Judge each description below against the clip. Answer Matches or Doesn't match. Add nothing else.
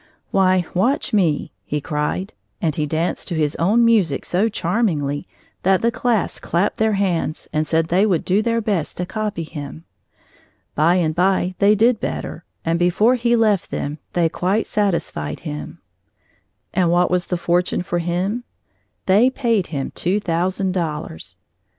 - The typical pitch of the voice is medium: Matches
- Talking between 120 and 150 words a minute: Doesn't match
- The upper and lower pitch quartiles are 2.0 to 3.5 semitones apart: Doesn't match